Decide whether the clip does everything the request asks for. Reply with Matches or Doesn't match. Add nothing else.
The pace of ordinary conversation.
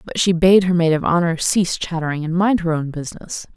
Doesn't match